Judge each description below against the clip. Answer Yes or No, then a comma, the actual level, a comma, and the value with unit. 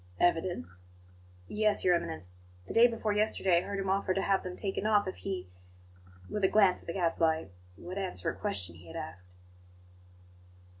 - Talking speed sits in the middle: Yes, average, 180 wpm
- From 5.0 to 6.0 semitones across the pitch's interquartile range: No, average, 3.6 semitones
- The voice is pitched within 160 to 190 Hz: Yes, medium, 185 Hz